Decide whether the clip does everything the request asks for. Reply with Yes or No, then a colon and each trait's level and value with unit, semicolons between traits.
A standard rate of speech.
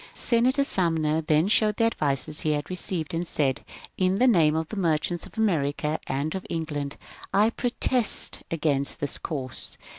Yes: average, 160 wpm